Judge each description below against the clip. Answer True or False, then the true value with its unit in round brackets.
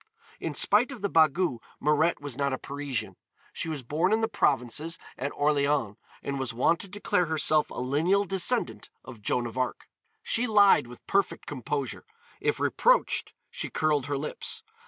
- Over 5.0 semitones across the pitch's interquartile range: True (5.5 semitones)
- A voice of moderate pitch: True (150 Hz)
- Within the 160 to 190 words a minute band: True (170 wpm)